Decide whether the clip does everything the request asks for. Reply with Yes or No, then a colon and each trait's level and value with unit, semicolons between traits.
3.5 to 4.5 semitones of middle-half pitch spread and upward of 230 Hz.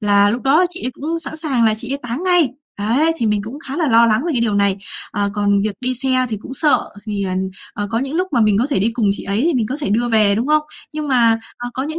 No: average, 5.2 semitones; high, 240 Hz